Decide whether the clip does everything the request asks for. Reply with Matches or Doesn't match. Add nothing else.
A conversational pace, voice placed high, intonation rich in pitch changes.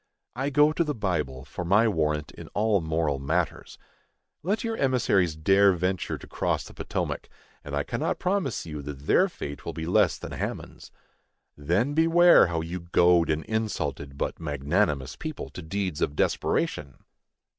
Doesn't match